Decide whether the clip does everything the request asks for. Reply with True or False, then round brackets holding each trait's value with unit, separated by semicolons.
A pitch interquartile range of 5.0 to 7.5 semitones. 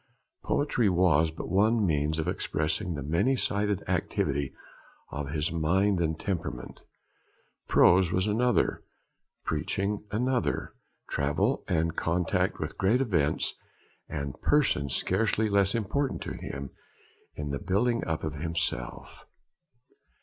True (5.3 semitones)